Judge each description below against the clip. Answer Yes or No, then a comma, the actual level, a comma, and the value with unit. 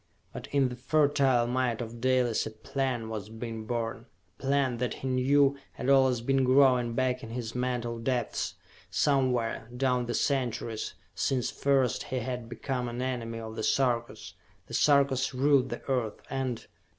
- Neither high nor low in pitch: No, low, 125 Hz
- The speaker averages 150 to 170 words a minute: Yes, average, 160 wpm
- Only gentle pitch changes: Yes, narrow, 2.2 semitones